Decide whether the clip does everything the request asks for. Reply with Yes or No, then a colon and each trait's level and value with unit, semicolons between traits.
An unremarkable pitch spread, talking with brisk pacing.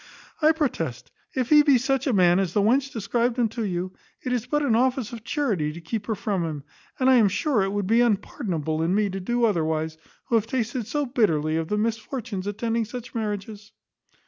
Yes: average, 4.8 semitones; fast, 215 wpm